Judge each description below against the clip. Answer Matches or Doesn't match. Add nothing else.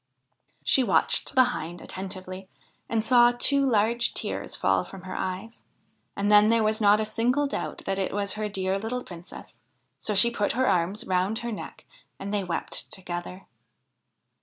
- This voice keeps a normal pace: Matches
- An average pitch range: Matches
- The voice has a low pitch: Doesn't match